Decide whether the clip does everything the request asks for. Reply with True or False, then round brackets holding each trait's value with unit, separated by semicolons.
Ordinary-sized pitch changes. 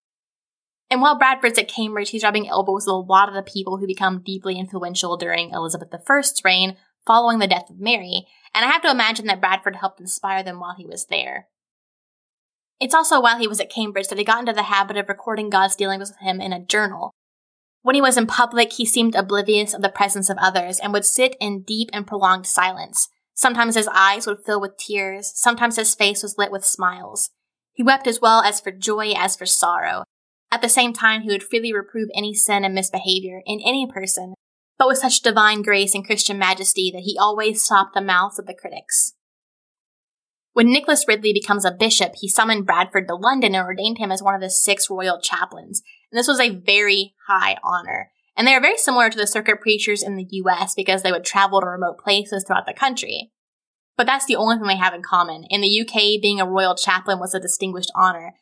True (3.0 semitones)